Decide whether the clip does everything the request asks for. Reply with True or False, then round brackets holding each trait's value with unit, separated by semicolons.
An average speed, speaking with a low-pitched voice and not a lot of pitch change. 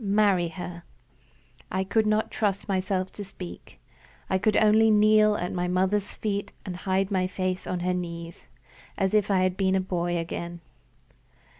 False (165 wpm; 190 Hz; 2.3 semitones)